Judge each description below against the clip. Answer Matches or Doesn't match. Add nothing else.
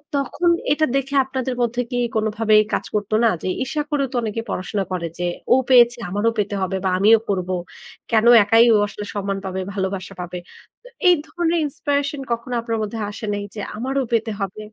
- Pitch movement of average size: Matches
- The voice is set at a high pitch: Matches